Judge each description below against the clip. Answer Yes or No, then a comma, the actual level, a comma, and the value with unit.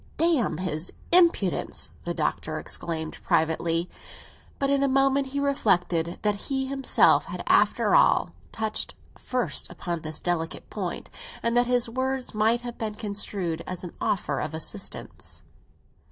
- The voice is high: Yes, high, 215 Hz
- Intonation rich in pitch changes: Yes, wide, 7.5 semitones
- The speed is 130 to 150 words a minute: Yes, average, 140 wpm